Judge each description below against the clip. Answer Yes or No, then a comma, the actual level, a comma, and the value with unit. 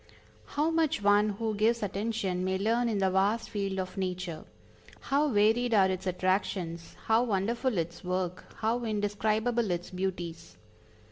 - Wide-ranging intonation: No, average, 3.4 semitones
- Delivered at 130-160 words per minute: Yes, average, 145 wpm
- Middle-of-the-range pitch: No, high, 205 Hz